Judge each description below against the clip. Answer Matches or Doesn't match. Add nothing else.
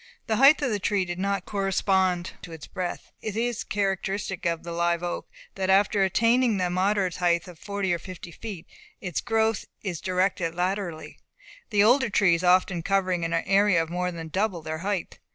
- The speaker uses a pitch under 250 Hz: Matches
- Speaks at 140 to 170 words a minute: Doesn't match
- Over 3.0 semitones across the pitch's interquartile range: Doesn't match